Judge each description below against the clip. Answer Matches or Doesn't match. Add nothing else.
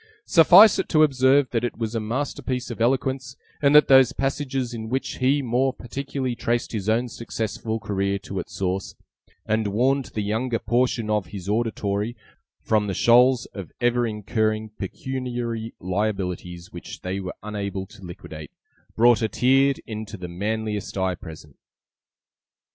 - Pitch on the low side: Matches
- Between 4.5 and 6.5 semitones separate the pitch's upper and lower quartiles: Doesn't match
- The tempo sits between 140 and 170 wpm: Matches